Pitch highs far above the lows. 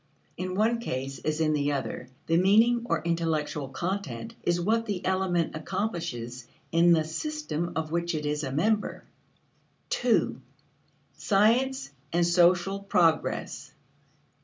No: average, 4.5 semitones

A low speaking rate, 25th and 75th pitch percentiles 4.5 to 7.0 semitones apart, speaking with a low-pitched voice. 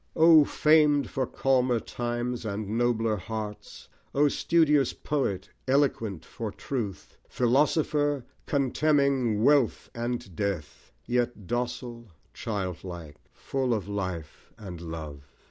Yes: slow, 105 wpm; average, 5.3 semitones; low, 120 Hz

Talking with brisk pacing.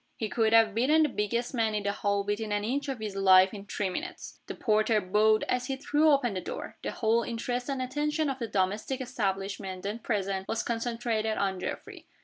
Yes: fast, 210 wpm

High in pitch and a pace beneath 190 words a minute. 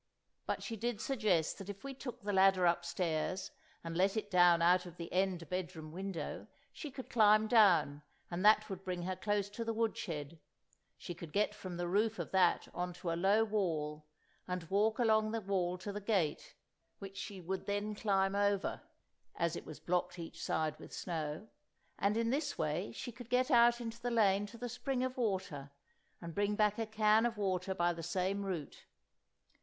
No: high, 195 Hz; average, 200 wpm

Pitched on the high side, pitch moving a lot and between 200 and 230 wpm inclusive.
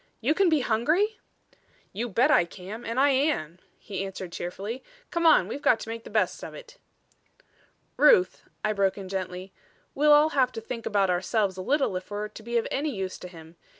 Yes: high, 225 Hz; wide, 7.0 semitones; fast, 205 wpm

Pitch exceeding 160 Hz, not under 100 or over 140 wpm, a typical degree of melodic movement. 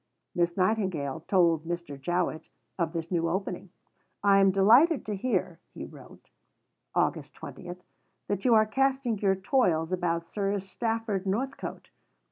Yes: high, 190 Hz; slow, 135 wpm; average, 4.0 semitones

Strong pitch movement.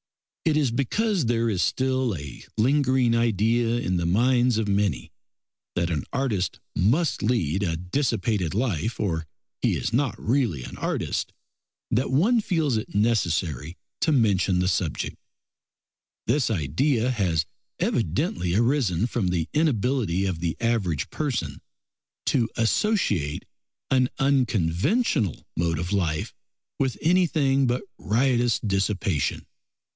Yes: wide, 6.6 semitones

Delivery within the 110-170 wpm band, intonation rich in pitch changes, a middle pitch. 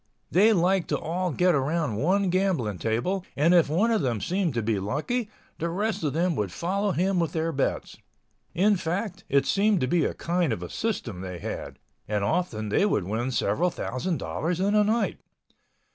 No: average, 190 wpm; wide, 7.3 semitones; medium, 170 Hz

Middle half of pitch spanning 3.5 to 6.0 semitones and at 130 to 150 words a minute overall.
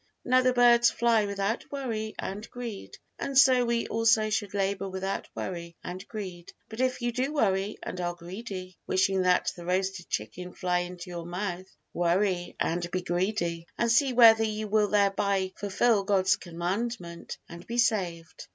No: average, 4.0 semitones; average, 165 wpm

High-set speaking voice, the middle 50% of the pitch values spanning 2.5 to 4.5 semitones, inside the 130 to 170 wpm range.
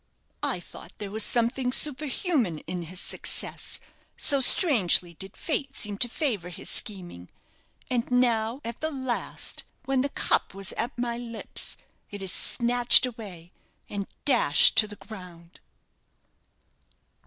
No: high, 230 Hz; average, 4.9 semitones; slow, 135 wpm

